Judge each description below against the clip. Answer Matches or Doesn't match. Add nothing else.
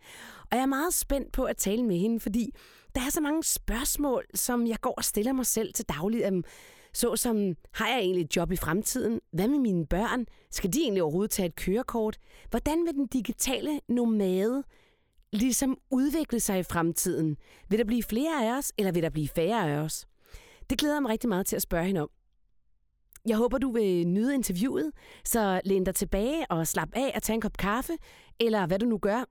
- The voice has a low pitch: Doesn't match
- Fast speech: Doesn't match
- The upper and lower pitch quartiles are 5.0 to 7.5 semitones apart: Matches